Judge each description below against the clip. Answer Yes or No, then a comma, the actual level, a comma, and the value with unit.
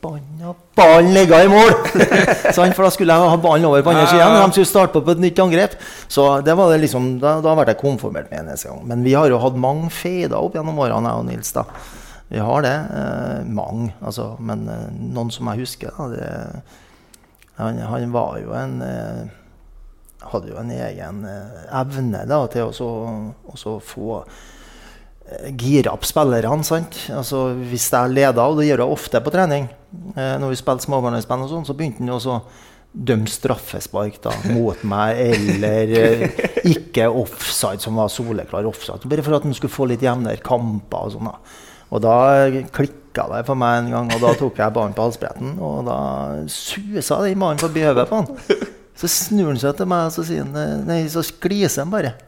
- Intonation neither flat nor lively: No, wide, 5.8 semitones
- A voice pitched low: Yes, low, 130 Hz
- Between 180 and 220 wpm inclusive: Yes, average, 185 wpm